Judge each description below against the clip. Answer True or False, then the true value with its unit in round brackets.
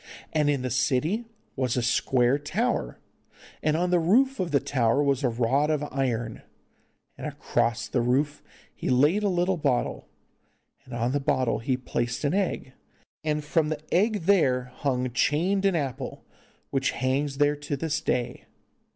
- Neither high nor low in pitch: True (145 Hz)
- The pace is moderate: True (160 wpm)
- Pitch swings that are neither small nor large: True (4.1 semitones)